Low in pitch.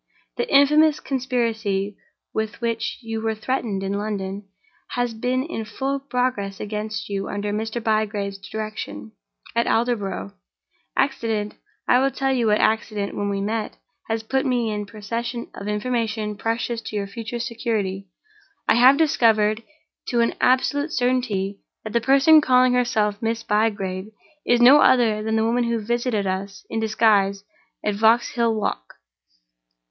No: high, 225 Hz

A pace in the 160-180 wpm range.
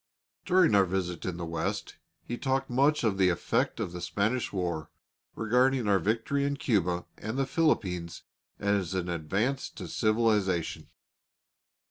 No: average, 145 wpm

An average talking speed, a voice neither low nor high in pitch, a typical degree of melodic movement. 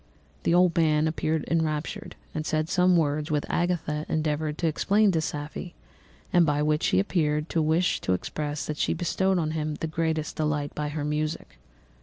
No: average, 180 wpm; medium, 155 Hz; narrow, 1.7 semitones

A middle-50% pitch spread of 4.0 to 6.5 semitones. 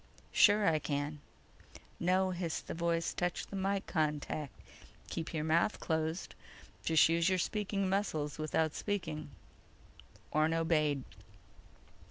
No: average, 3.3 semitones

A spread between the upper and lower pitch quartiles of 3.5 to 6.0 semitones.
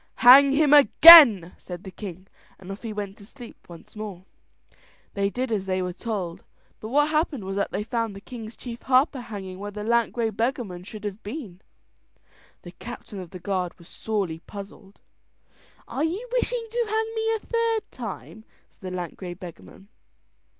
Yes: wide, 5.5 semitones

